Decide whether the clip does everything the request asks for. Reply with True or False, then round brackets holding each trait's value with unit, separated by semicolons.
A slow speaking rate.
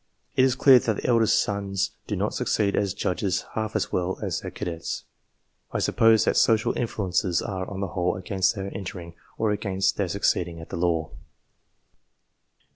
False (175 wpm)